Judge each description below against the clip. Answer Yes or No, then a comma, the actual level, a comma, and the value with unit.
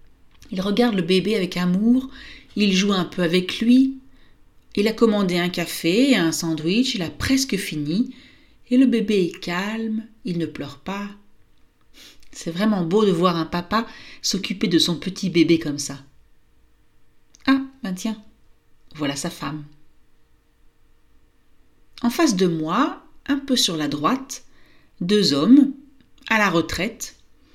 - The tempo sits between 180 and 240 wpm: No, slow, 145 wpm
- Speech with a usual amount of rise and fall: No, wide, 6.0 semitones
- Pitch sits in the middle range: No, high, 200 Hz